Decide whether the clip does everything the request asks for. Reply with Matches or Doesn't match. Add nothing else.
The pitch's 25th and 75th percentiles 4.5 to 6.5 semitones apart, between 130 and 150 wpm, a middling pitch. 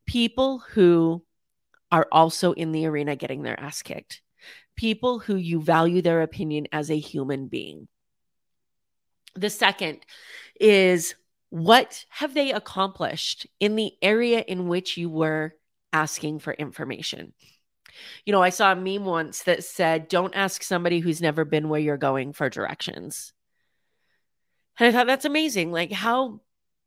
Matches